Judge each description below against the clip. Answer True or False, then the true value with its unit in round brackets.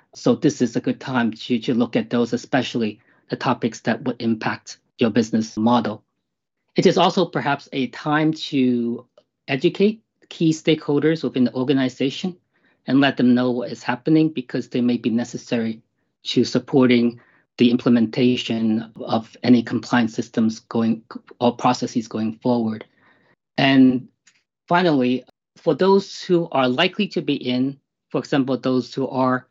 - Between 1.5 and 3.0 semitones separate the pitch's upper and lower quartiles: False (4.3 semitones)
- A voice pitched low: True (125 Hz)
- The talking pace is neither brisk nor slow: True (150 wpm)